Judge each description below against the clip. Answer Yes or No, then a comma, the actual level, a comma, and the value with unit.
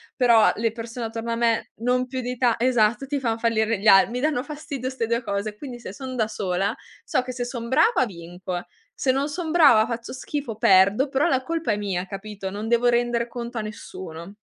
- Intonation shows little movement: No, average, 3.3 semitones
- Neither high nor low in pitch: No, high, 235 Hz